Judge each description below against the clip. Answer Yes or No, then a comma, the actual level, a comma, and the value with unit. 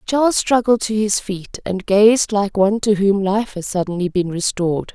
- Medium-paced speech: Yes, average, 195 wpm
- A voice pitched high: Yes, high, 200 Hz